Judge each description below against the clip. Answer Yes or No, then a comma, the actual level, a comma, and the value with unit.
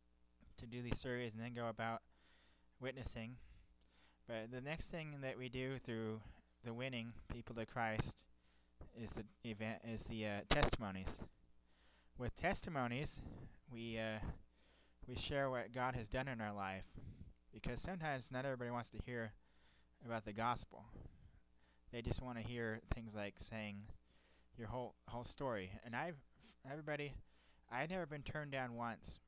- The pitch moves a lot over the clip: Yes, wide, 6.8 semitones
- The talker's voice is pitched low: Yes, low, 115 Hz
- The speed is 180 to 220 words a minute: No, average, 150 wpm